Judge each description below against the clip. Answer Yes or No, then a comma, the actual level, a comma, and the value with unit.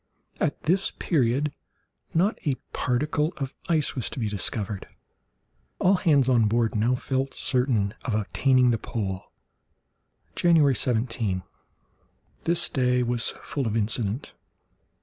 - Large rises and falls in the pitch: No, average, 4.4 semitones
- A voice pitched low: Yes, low, 125 Hz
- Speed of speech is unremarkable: No, slow, 120 wpm